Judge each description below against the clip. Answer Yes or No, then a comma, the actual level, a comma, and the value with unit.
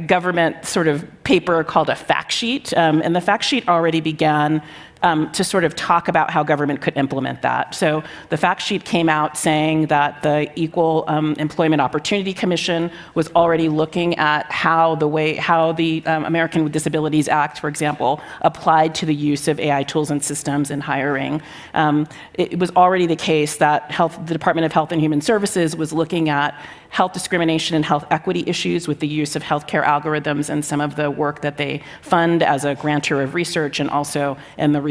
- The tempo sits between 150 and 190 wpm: No, average, 200 wpm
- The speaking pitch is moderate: Yes, medium, 155 Hz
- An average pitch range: No, narrow, 2.1 semitones